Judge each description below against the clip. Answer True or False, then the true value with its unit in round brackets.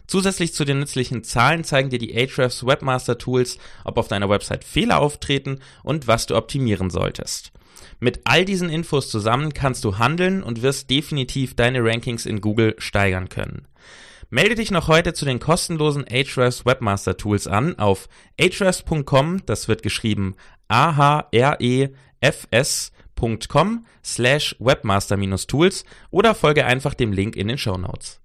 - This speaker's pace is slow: False (140 wpm)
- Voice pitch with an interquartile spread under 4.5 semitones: False (5.1 semitones)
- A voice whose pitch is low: True (130 Hz)